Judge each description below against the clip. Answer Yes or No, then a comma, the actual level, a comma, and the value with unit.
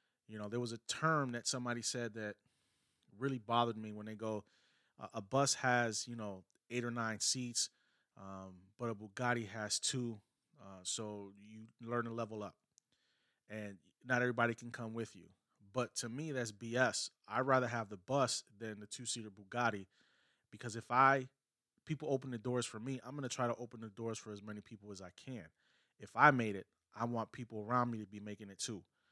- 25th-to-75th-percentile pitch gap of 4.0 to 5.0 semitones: No, average, 2.7 semitones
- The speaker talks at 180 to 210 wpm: Yes, average, 200 wpm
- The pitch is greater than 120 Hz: No, low, 115 Hz